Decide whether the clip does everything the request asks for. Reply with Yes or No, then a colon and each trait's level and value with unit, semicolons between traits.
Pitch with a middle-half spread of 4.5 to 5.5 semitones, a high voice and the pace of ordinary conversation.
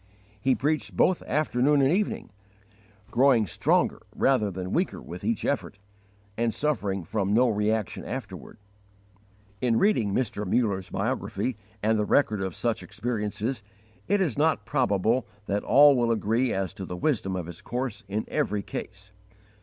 No: average, 4.8 semitones; low, 115 Hz; average, 150 wpm